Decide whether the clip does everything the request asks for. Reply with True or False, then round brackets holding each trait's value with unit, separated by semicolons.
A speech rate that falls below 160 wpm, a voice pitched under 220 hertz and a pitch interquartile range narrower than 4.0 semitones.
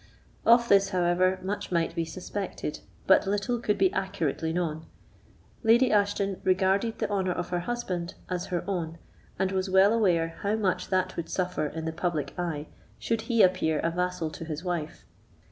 False (175 wpm; 185 Hz; 3.0 semitones)